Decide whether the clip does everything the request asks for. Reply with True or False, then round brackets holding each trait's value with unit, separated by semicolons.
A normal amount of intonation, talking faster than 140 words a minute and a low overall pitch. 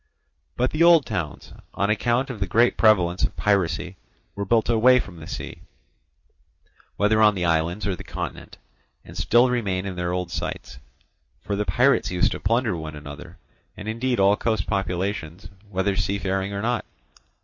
True (4.0 semitones; 170 wpm; 100 Hz)